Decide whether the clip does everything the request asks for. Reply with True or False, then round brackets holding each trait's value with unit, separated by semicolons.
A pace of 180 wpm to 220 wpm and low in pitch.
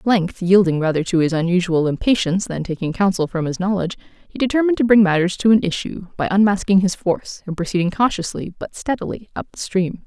False (205 wpm; 185 Hz)